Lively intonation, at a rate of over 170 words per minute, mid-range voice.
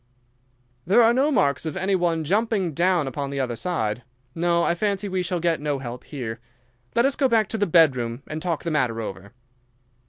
Yes: wide, 5.9 semitones; average, 200 wpm; medium, 170 Hz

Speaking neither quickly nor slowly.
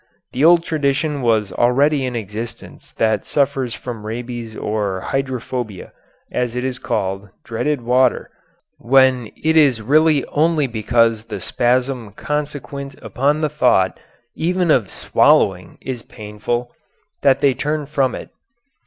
No: slow, 130 wpm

